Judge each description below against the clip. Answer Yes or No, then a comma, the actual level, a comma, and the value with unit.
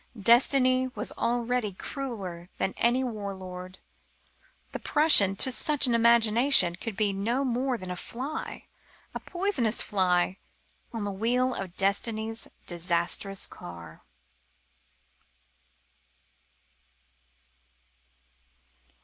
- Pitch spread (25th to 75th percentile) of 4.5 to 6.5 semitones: Yes, average, 4.8 semitones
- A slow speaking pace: Yes, slow, 100 wpm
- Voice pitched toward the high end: Yes, high, 225 Hz